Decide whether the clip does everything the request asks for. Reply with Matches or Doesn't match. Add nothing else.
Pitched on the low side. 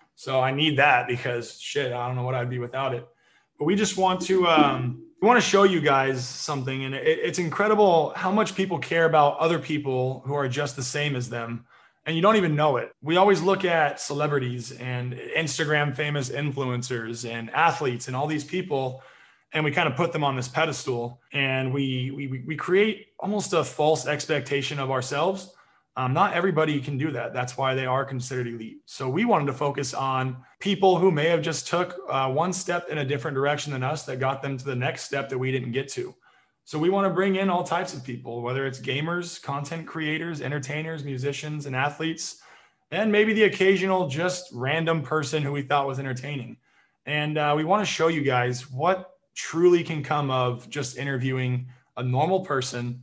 Doesn't match